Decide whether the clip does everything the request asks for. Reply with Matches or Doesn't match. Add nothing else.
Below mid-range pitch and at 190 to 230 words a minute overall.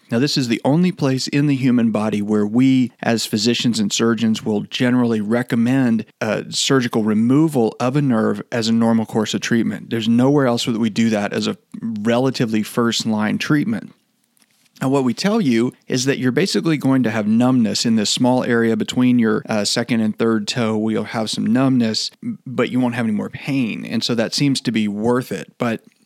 Matches